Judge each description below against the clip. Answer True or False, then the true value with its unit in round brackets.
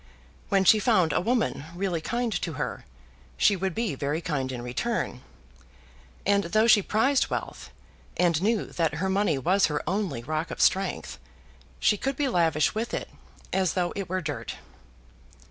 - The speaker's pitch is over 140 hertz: True (185 Hz)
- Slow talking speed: False (165 wpm)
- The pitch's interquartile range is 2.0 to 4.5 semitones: False (5.1 semitones)